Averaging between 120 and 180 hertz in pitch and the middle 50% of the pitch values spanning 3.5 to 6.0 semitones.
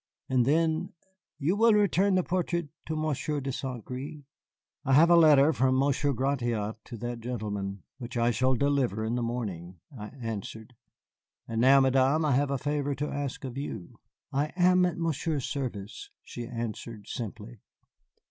Yes: low, 135 Hz; average, 4.3 semitones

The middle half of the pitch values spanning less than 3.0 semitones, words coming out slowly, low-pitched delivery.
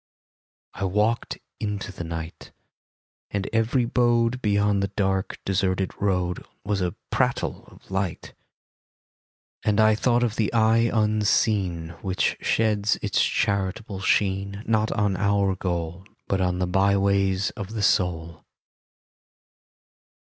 Yes: narrow, 2.4 semitones; slow, 125 wpm; low, 100 Hz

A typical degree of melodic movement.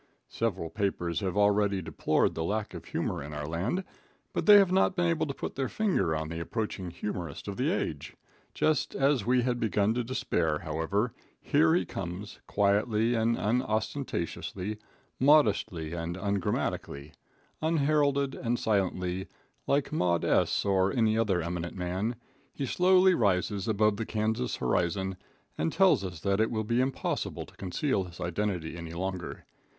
No: wide, 5.9 semitones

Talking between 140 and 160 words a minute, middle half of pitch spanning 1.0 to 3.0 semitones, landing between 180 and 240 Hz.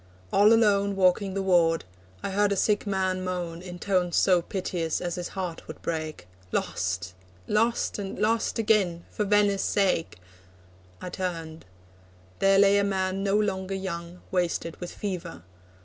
Yes: average, 150 wpm; narrow, 2.5 semitones; high, 190 Hz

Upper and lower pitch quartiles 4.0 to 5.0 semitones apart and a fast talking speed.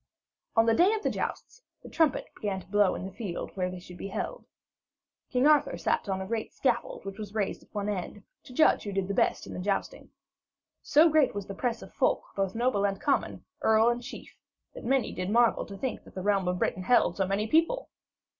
Yes: average, 4.4 semitones; fast, 225 wpm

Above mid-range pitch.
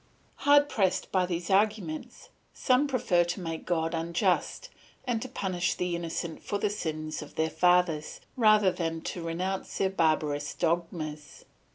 No: medium, 175 Hz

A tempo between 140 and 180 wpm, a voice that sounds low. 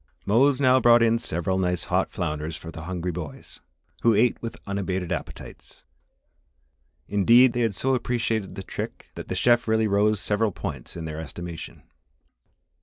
Yes: average, 160 wpm; low, 100 Hz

